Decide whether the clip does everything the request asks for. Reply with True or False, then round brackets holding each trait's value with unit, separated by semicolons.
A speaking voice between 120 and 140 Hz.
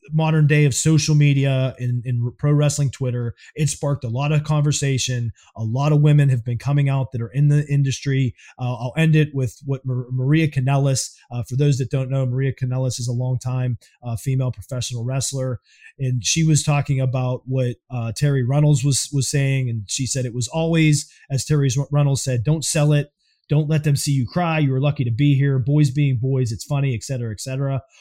True (135 Hz)